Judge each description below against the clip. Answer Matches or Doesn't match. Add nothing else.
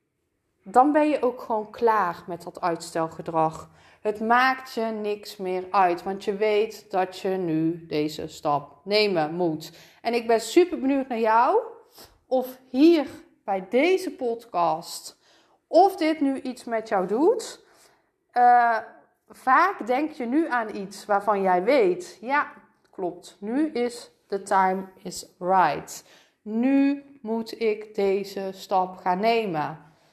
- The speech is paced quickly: Doesn't match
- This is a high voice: Matches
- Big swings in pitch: Matches